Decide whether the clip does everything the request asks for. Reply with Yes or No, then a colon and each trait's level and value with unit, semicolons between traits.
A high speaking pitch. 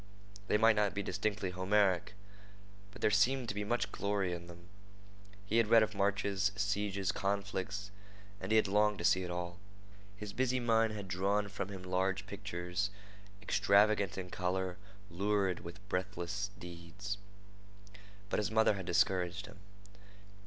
No: low, 100 Hz